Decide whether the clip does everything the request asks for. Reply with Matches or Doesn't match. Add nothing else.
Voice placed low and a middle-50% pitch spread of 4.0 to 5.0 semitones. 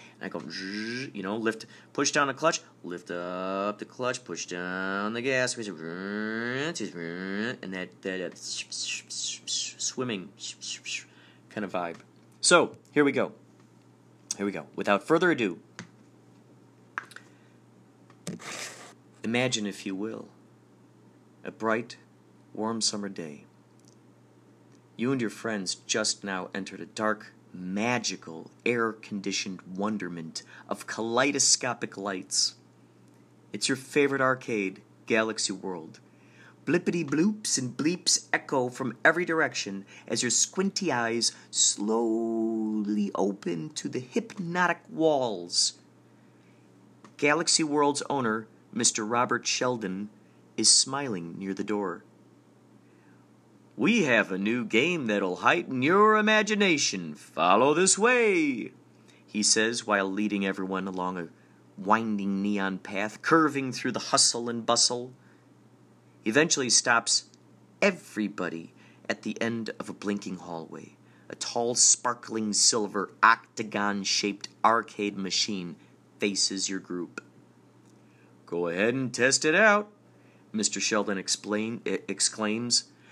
Matches